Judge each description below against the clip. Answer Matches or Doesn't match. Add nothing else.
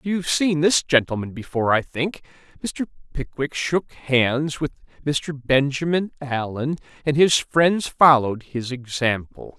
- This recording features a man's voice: Matches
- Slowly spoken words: Matches